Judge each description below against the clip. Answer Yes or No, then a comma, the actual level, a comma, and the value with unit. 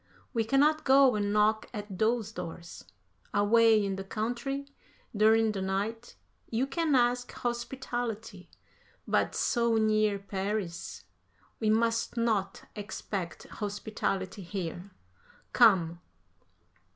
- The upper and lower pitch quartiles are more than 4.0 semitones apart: No, average, 3.1 semitones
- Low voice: No, high, 215 Hz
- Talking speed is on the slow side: Yes, slow, 105 wpm